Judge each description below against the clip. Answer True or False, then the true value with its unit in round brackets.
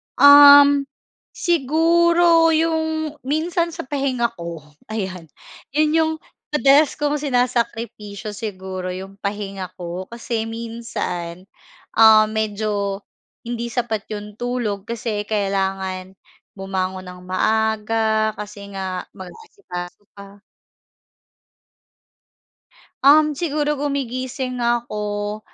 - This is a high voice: True (220 Hz)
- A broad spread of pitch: True (6.2 semitones)